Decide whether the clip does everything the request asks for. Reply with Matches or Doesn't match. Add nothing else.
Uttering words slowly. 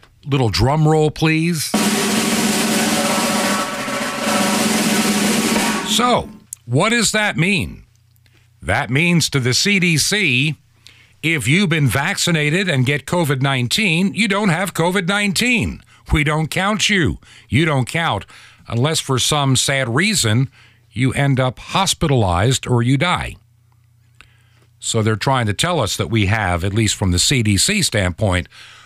Matches